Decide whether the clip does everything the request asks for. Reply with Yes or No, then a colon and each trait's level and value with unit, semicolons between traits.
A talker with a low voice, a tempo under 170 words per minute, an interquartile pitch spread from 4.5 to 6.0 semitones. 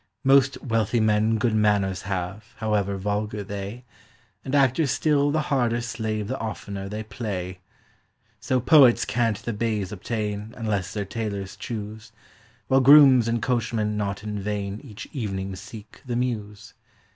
No: low, 110 Hz; average, 145 wpm; average, 2.8 semitones